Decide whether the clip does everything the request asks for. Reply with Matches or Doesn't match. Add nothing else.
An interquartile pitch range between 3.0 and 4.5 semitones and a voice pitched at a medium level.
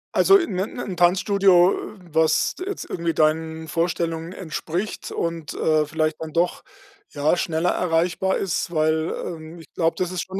Doesn't match